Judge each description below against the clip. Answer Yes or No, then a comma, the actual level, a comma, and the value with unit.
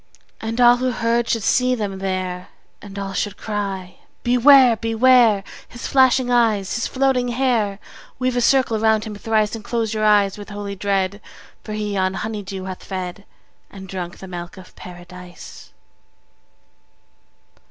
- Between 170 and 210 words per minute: No, average, 160 wpm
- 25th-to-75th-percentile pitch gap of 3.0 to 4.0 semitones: Yes, average, 3.7 semitones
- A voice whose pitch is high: Yes, high, 210 Hz